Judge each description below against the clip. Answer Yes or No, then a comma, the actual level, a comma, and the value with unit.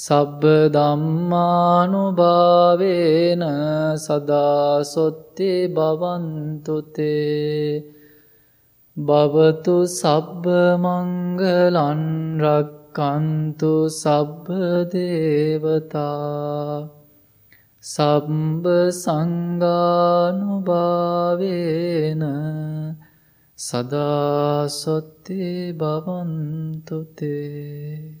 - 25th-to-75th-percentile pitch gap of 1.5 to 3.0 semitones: Yes, average, 2.7 semitones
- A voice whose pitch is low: No, medium, 155 Hz